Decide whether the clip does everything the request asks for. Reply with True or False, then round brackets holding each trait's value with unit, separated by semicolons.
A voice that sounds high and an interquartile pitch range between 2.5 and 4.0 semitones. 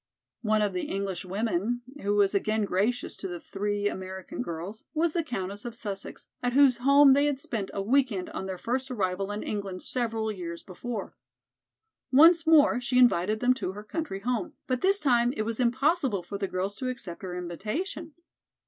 False (215 Hz; 4.7 semitones)